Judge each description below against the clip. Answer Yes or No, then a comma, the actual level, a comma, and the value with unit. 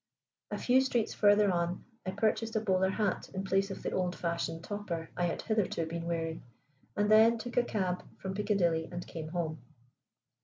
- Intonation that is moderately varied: Yes, average, 3.8 semitones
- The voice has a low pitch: No, high, 190 Hz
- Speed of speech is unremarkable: Yes, average, 185 wpm